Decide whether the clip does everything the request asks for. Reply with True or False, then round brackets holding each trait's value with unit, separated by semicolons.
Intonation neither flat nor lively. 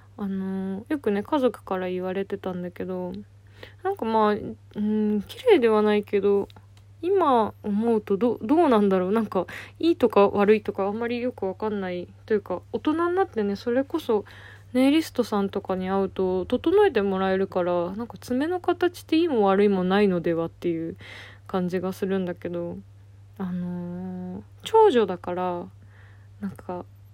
True (4.1 semitones)